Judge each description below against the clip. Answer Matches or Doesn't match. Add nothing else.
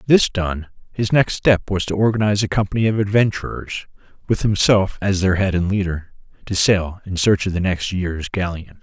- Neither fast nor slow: Matches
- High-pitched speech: Doesn't match